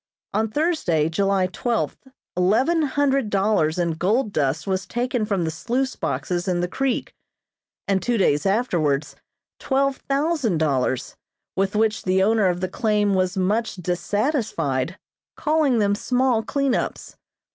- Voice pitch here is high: Yes, high, 205 Hz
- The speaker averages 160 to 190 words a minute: No, average, 140 wpm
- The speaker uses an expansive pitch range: Yes, wide, 5.7 semitones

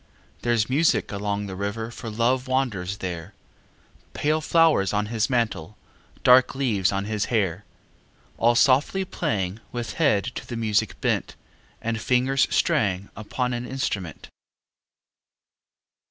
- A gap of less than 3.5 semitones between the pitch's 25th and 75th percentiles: No, average, 4.2 semitones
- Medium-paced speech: No, slow, 125 wpm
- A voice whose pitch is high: No, low, 115 Hz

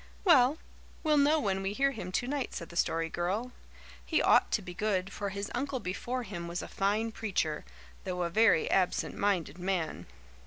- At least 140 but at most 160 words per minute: No, average, 185 wpm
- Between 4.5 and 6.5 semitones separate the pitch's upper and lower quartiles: Yes, wide, 5.5 semitones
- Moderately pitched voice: No, high, 200 Hz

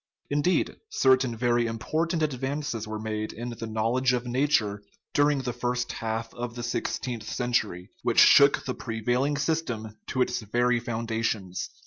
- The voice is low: Yes, low, 120 Hz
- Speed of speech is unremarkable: Yes, average, 150 wpm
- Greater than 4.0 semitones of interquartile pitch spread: No, average, 2.8 semitones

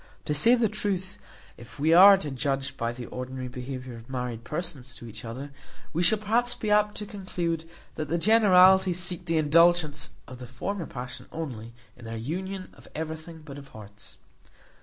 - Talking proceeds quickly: No, average, 180 wpm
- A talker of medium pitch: Yes, medium, 155 Hz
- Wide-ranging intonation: Yes, wide, 6.6 semitones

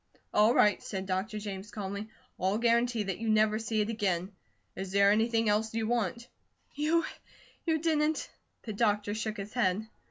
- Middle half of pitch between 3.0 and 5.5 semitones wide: No, narrow, 2.5 semitones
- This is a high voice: Yes, high, 215 Hz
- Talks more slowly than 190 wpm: Yes, average, 170 wpm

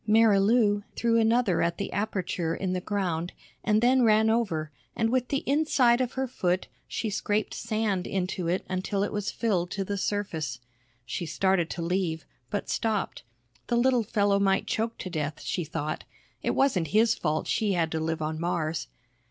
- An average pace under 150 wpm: No, average, 175 wpm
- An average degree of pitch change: Yes, average, 4.6 semitones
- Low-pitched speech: No, high, 200 Hz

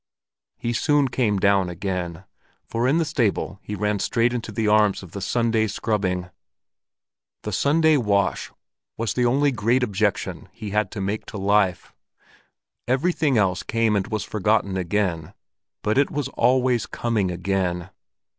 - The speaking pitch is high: No, low, 105 Hz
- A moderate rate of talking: Yes, average, 150 wpm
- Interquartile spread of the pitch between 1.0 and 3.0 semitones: No, average, 3.9 semitones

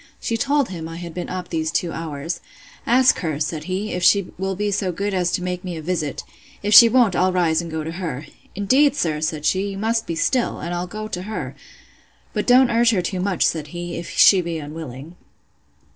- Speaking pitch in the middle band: Yes, medium, 180 Hz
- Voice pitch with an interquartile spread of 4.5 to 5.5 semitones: No, average, 3.9 semitones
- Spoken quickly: Yes, fast, 225 wpm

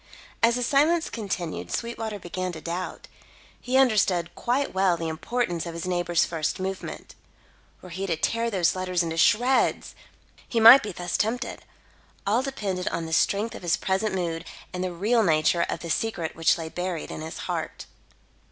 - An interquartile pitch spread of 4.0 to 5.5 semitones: Yes, average, 5.1 semitones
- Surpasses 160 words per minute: Yes, average, 175 wpm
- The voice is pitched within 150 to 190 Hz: Yes, medium, 185 Hz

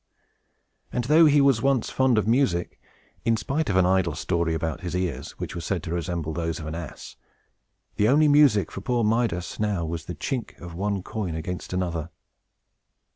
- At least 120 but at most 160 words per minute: No, average, 185 wpm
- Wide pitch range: Yes, wide, 6.1 semitones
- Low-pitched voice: Yes, very low, 95 Hz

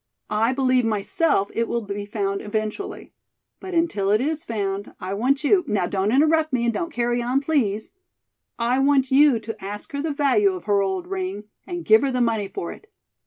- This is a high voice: Yes, high, 235 Hz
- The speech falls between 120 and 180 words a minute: No, average, 200 wpm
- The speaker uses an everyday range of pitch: No, wide, 5.8 semitones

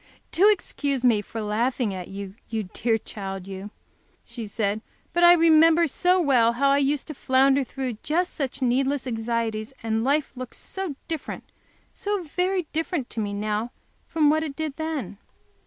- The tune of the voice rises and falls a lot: Yes, wide, 6.1 semitones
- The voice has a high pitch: Yes, very high, 265 Hz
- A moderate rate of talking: Yes, average, 170 wpm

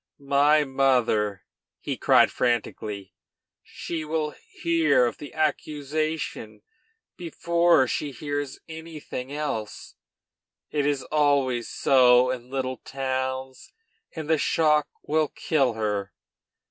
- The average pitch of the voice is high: No, medium, 140 Hz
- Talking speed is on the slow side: Yes, slow, 105 wpm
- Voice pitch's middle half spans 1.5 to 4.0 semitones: Yes, average, 3.4 semitones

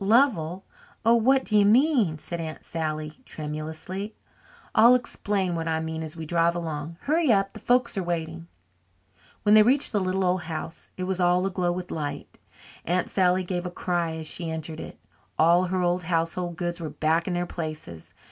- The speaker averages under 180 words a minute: No, average, 185 wpm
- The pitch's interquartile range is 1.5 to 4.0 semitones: Yes, average, 3.2 semitones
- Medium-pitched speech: Yes, medium, 175 Hz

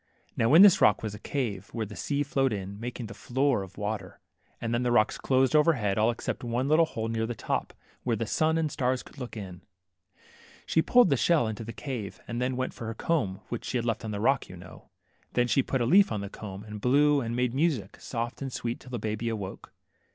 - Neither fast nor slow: No, fast, 245 wpm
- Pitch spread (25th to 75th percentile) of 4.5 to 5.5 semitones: No, average, 4.0 semitones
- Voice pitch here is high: No, low, 120 Hz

